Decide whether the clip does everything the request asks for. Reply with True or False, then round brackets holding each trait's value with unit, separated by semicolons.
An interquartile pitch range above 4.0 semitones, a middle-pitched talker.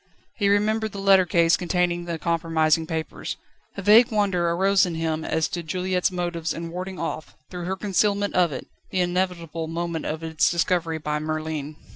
False (2.6 semitones; 175 Hz)